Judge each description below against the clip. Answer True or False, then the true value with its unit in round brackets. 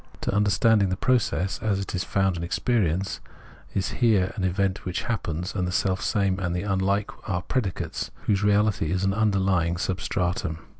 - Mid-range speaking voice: False (95 Hz)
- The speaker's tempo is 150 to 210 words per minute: True (170 wpm)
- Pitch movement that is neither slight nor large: False (2.1 semitones)